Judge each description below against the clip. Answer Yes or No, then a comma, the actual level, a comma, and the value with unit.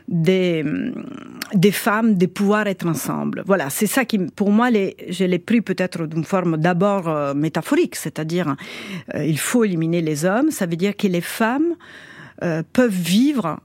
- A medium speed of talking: Yes, average, 170 wpm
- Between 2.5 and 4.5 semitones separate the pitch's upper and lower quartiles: No, average, 4.9 semitones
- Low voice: No, high, 190 Hz